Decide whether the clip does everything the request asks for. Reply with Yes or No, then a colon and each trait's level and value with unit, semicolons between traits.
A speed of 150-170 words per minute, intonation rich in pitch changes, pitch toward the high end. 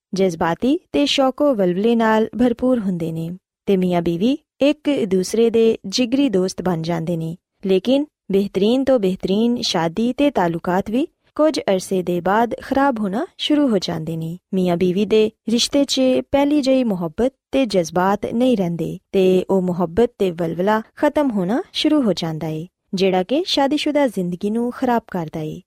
Yes: average, 160 wpm; wide, 6.2 semitones; high, 210 Hz